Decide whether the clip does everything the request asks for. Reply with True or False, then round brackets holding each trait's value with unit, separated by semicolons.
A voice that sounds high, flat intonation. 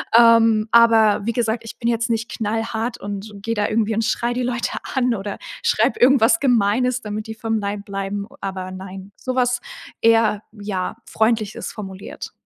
True (220 Hz; 2.3 semitones)